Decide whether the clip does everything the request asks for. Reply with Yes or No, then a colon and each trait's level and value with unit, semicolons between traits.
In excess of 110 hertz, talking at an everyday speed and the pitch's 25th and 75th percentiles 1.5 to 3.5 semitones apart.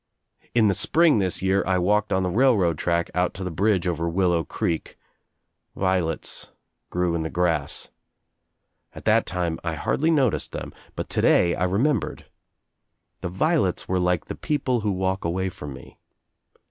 No: very low, 95 Hz; average, 160 wpm; average, 3.2 semitones